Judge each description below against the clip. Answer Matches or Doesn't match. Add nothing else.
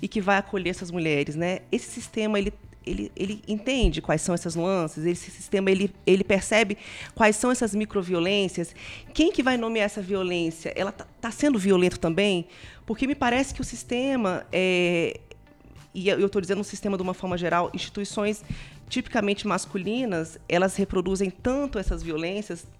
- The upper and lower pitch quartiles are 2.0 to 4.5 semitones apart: Matches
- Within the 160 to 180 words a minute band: Matches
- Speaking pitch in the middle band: Doesn't match